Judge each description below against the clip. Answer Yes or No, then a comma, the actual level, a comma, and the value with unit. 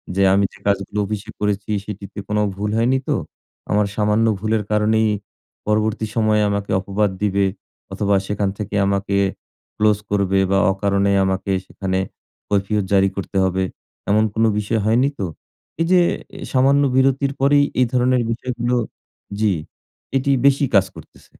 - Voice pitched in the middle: No, low, 105 Hz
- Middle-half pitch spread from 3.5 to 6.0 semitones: No, average, 2.7 semitones